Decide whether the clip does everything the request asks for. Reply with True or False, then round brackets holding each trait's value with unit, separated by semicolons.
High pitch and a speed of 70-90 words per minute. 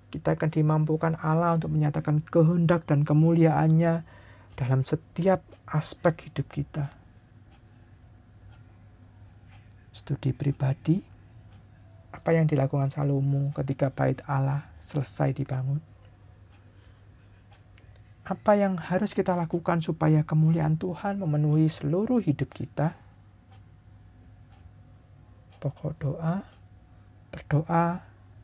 False (140 Hz; 85 wpm)